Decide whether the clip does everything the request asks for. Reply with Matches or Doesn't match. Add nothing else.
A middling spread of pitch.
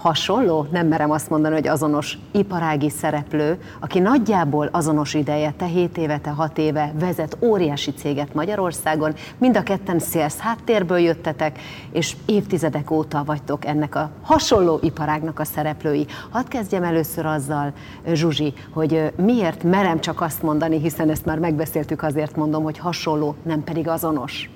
Doesn't match